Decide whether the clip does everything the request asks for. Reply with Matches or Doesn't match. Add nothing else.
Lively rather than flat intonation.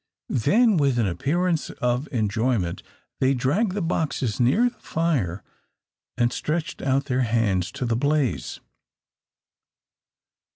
Matches